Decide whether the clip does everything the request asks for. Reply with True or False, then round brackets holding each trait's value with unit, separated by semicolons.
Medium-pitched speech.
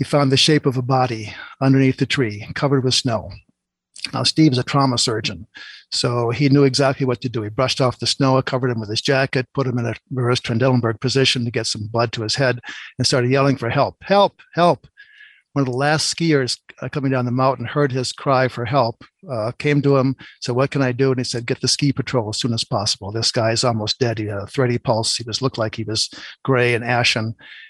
False (130 Hz)